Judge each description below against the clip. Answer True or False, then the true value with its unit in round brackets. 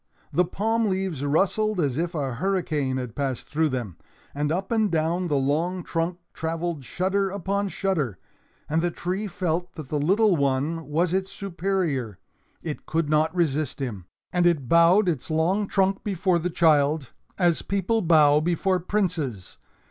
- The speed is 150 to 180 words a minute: True (160 wpm)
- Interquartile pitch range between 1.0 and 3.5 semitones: False (4.3 semitones)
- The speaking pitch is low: False (170 Hz)